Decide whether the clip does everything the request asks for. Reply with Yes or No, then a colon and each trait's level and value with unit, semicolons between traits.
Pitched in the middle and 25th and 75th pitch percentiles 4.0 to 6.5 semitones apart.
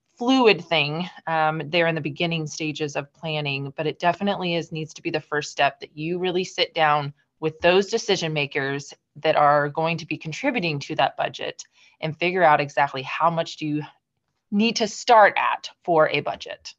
No: medium, 160 Hz; average, 3.1 semitones